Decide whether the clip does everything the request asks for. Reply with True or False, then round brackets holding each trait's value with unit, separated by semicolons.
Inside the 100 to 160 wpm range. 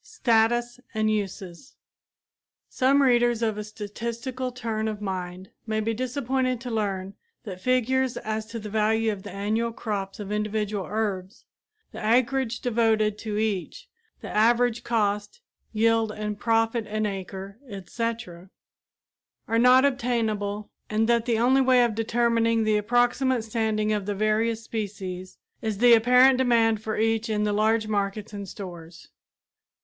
True (145 wpm)